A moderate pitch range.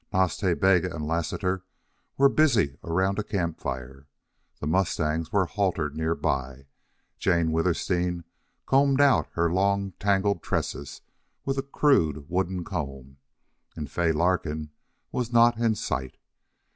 Yes: average, 4.3 semitones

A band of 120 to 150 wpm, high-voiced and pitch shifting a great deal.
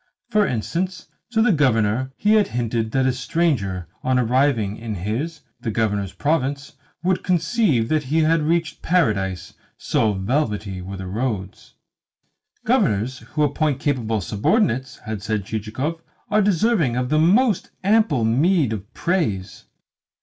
No: average, 140 wpm; low, 130 Hz; wide, 7.3 semitones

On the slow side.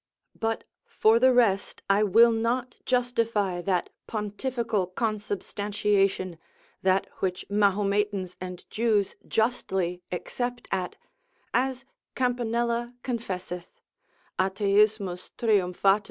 Yes: slow, 90 wpm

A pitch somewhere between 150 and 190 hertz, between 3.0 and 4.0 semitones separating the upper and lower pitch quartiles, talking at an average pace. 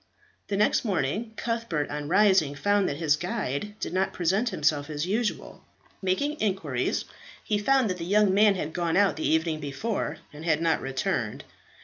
No: medium, 185 Hz; wide, 5.4 semitones; average, 170 wpm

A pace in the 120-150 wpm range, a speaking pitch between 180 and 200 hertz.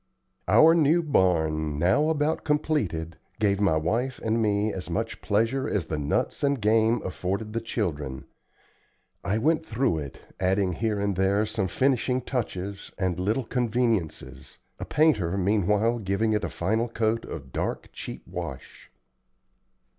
No: average, 145 wpm; low, 105 Hz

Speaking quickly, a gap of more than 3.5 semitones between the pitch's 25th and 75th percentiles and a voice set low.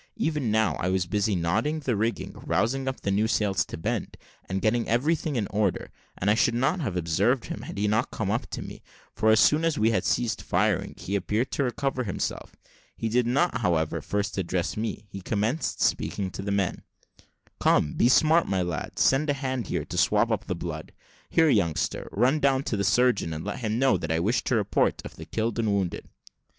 Yes: fast, 210 wpm; average, 4.7 semitones; low, 110 Hz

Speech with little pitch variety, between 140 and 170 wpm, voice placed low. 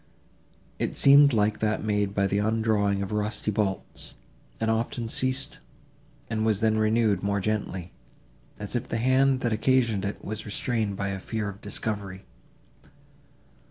Yes: narrow, 2.1 semitones; average, 150 wpm; low, 110 Hz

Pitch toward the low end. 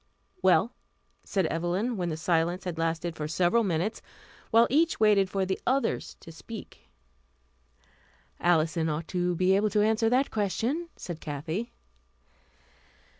No: medium, 185 Hz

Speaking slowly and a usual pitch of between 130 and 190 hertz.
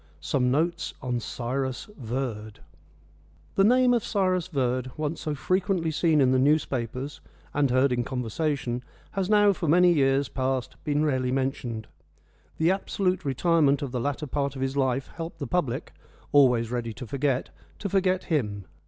No: average, 160 wpm; medium, 140 Hz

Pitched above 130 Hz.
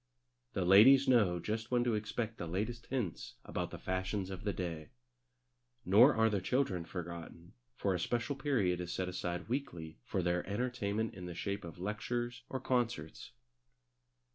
No: low, 100 Hz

